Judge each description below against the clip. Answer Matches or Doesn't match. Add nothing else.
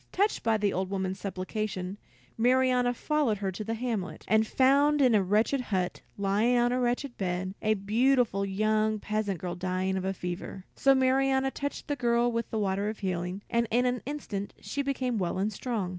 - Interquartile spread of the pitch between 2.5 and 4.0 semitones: Doesn't match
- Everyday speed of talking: Matches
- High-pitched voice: Matches